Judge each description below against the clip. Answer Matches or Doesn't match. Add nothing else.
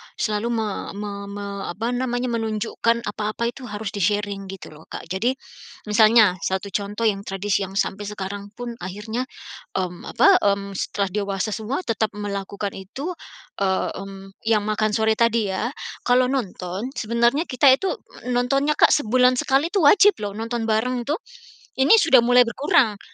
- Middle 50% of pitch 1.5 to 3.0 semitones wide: Doesn't match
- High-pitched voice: Matches